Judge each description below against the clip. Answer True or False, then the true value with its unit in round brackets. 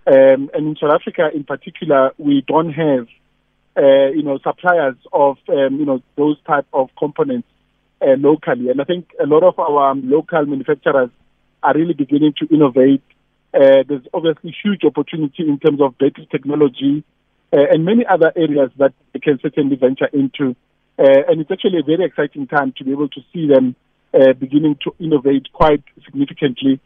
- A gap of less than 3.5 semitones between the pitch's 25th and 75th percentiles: True (2.8 semitones)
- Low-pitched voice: False (150 Hz)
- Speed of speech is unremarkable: True (175 wpm)